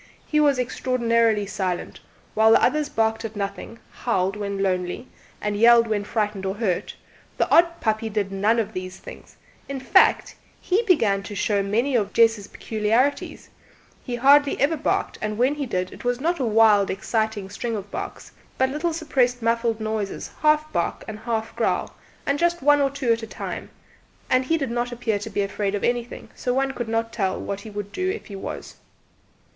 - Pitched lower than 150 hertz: No, high, 225 Hz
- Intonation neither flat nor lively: Yes, average, 4.1 semitones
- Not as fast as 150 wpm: No, average, 190 wpm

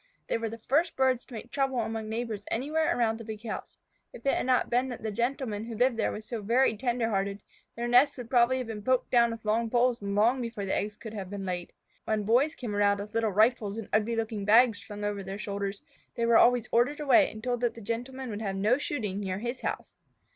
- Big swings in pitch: No, average, 2.8 semitones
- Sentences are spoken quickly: Yes, fast, 245 wpm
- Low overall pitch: No, high, 230 Hz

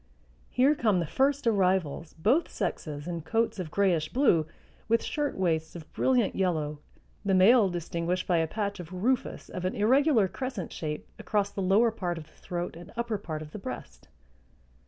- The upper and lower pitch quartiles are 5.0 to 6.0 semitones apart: Yes, wide, 5.4 semitones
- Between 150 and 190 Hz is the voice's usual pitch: Yes, medium, 185 Hz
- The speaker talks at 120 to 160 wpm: No, average, 175 wpm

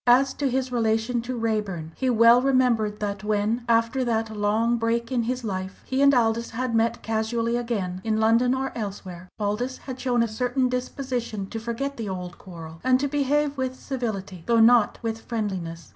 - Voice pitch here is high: Yes, high, 230 Hz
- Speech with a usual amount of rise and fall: Yes, average, 3.0 semitones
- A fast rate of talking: No, average, 185 wpm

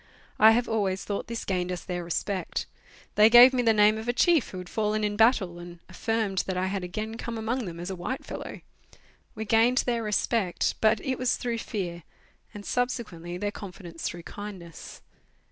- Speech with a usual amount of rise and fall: Yes, average, 3.9 semitones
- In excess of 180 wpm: Yes, average, 195 wpm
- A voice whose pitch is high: Yes, high, 210 Hz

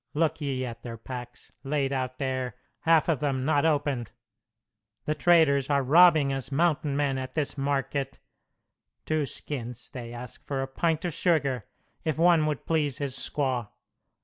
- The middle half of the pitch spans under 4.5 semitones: Yes, average, 2.9 semitones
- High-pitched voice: No, medium, 140 Hz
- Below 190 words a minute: Yes, average, 160 wpm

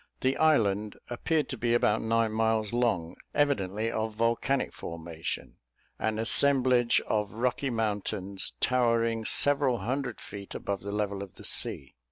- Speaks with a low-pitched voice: Yes, low, 115 Hz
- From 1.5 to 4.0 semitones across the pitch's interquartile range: Yes, average, 3.4 semitones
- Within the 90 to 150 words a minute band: Yes, average, 140 wpm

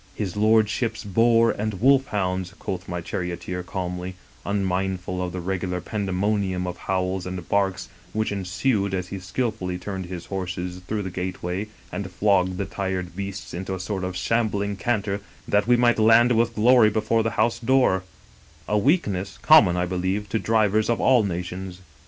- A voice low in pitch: Yes, very low, 95 Hz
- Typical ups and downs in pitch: Yes, average, 3.0 semitones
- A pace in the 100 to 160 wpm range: No, average, 170 wpm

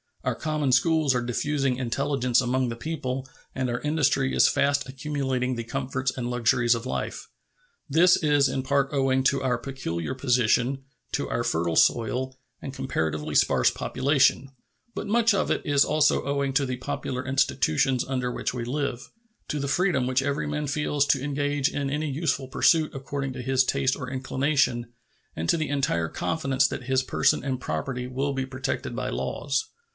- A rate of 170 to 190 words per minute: Yes, average, 175 wpm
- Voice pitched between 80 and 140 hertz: Yes, low, 135 Hz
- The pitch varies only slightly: Yes, narrow, 2.0 semitones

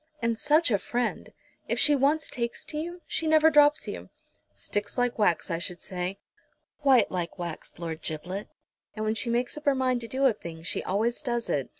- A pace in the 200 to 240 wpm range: Yes, fast, 205 wpm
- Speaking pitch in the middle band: No, high, 235 Hz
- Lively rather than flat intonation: Yes, wide, 7.2 semitones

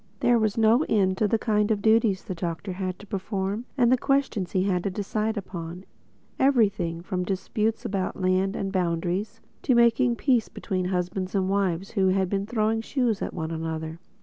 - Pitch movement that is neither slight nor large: Yes, average, 3.3 semitones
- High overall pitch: Yes, high, 195 Hz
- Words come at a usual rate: Yes, average, 185 wpm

